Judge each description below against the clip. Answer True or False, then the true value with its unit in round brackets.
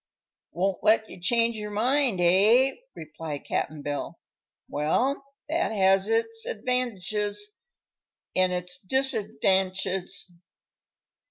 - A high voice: True (205 Hz)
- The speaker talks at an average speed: False (95 wpm)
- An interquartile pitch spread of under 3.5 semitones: False (4.0 semitones)